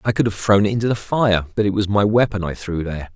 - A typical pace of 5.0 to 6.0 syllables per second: No, 6.4 syllables/s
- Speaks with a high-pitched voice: No, low, 100 Hz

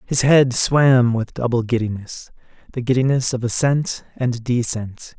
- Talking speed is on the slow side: Yes, slow, 125 wpm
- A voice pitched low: Yes, low, 125 Hz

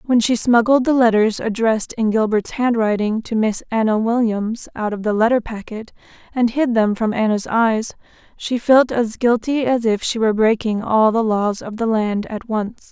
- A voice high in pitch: Yes, high, 225 Hz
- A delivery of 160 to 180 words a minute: No, average, 190 wpm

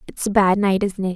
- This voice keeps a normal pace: No, fast, 315 wpm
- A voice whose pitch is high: Yes, high, 195 Hz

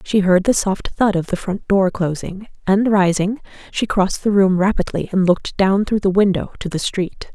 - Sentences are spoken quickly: Yes, fast, 210 wpm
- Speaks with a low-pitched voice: No, high, 195 Hz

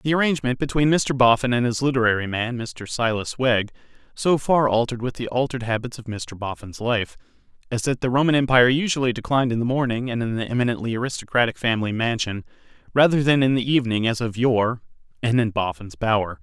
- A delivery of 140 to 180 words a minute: No, average, 190 wpm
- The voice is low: Yes, low, 120 Hz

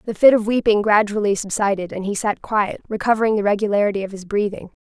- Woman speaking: Yes, female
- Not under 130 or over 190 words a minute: No, average, 200 wpm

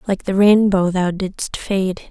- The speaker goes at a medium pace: Yes, average, 170 wpm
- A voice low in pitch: No, high, 190 Hz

